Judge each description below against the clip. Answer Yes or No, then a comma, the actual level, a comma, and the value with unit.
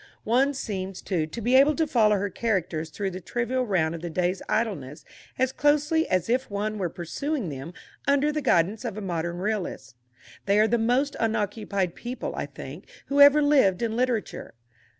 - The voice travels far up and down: Yes, wide, 6.0 semitones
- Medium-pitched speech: No, high, 215 Hz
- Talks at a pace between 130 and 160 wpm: No, average, 185 wpm